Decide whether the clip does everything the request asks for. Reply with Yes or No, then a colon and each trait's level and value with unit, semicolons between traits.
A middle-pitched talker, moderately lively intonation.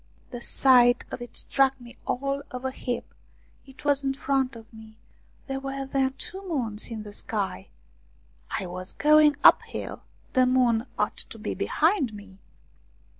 No: very high, 255 Hz; average, 3.4 semitones